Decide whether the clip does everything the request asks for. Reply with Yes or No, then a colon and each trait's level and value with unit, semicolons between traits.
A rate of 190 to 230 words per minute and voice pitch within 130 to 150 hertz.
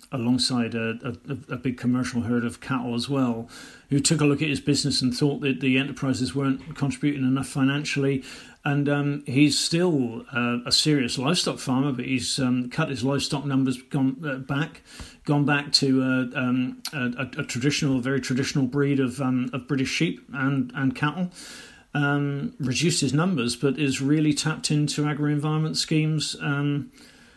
No: average, 180 wpm; low, 135 Hz